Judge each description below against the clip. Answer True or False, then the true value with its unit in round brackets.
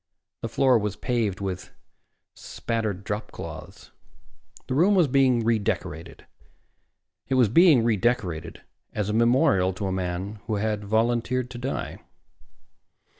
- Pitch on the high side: False (110 Hz)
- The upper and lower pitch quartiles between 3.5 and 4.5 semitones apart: True (3.9 semitones)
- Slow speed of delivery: True (125 wpm)